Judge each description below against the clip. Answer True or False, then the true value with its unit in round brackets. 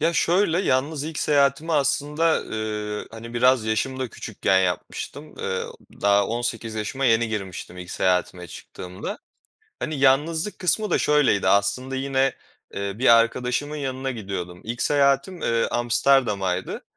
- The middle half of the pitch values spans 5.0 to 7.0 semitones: True (5.3 semitones)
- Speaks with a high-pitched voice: False (125 Hz)